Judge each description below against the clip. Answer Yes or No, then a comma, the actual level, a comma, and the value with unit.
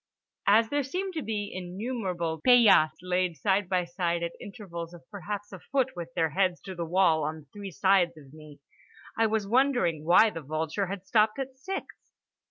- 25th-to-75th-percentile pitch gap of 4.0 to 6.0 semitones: Yes, average, 4.5 semitones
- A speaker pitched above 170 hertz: Yes, high, 190 Hz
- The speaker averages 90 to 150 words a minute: No, average, 180 wpm